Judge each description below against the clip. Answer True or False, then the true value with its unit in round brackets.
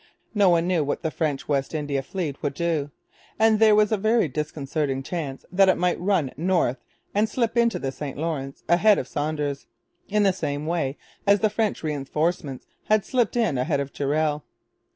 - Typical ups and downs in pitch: False (5.8 semitones)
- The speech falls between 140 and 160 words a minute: False (190 wpm)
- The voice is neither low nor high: True (160 Hz)